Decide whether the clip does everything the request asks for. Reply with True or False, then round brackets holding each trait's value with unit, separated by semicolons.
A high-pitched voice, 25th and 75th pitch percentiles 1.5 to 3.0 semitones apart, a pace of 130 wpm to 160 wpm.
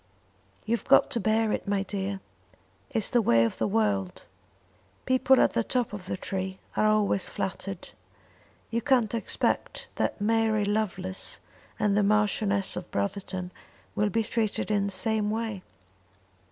True (210 Hz; 2.4 semitones; 150 wpm)